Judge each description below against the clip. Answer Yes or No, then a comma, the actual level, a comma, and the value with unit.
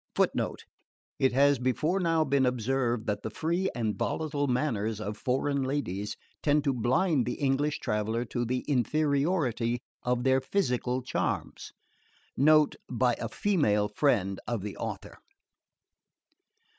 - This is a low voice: Yes, low, 130 Hz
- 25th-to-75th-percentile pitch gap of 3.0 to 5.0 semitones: Yes, average, 3.8 semitones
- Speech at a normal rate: No, slow, 130 wpm